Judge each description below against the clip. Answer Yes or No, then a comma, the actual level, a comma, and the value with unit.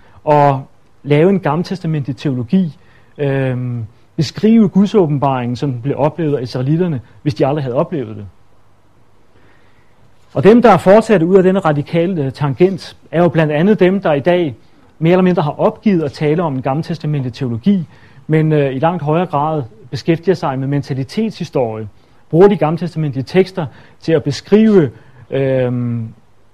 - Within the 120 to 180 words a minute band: Yes, average, 150 wpm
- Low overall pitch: No, medium, 145 Hz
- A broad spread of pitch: Yes, wide, 5.8 semitones